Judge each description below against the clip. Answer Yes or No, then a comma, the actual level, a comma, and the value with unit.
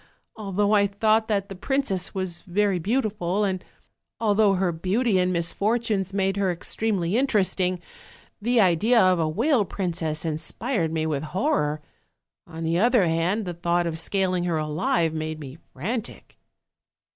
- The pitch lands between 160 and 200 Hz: Yes, medium, 185 Hz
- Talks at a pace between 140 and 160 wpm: Yes, average, 145 wpm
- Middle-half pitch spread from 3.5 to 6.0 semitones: Yes, average, 4.0 semitones